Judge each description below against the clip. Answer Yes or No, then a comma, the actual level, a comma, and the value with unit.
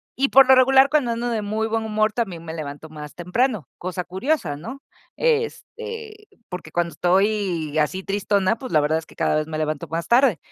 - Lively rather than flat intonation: Yes, wide, 7.8 semitones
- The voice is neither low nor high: No, high, 200 Hz